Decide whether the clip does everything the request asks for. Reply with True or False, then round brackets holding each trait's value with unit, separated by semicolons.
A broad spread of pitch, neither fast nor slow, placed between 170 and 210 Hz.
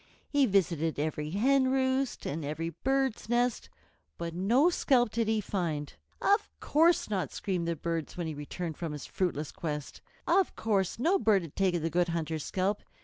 True (7.2 semitones; 175 wpm; 185 Hz)